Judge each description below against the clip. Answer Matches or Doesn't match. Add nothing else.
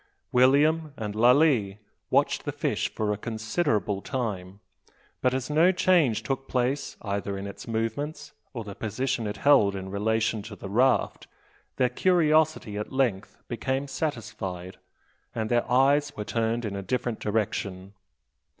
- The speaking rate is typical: Matches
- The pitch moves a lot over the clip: Doesn't match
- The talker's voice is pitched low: Matches